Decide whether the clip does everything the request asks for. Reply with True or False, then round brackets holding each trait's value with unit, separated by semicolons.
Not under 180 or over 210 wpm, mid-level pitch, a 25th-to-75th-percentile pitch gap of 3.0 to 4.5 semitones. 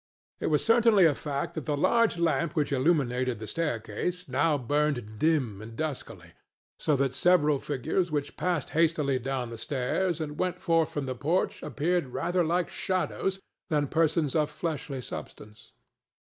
False (160 wpm; 150 Hz; 4.1 semitones)